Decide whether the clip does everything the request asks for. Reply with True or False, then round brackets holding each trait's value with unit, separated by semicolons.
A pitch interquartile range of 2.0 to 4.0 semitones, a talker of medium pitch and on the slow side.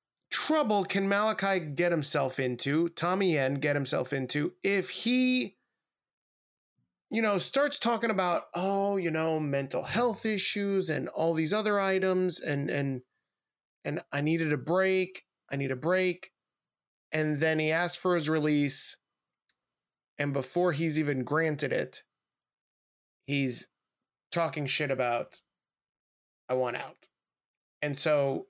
False (5.2 semitones; 160 Hz; 130 wpm)